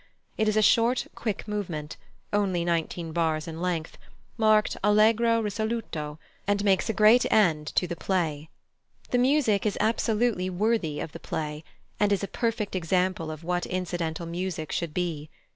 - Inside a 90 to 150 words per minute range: No, average, 160 wpm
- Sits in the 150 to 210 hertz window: Yes, medium, 185 Hz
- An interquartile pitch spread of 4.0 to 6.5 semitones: Yes, average, 4.7 semitones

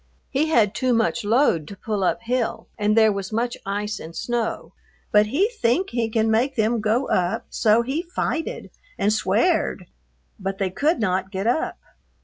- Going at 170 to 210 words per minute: Yes, average, 175 wpm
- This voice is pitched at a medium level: No, high, 225 Hz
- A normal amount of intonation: Yes, average, 3.2 semitones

